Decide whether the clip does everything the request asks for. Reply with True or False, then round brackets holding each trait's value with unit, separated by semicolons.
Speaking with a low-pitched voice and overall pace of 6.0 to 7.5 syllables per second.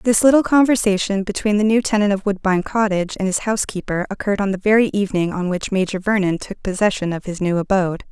False (200 Hz; 6.6 syllables/s)